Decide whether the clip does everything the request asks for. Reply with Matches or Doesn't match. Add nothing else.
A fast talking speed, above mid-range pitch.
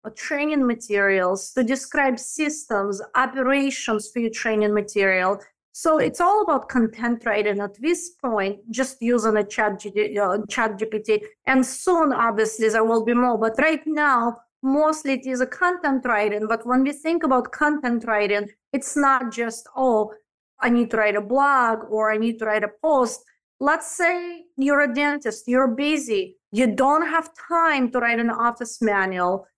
Doesn't match